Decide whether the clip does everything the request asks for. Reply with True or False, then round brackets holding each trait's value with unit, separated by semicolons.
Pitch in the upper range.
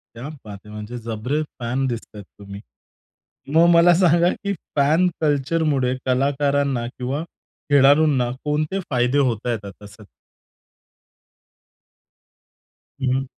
False (135 Hz)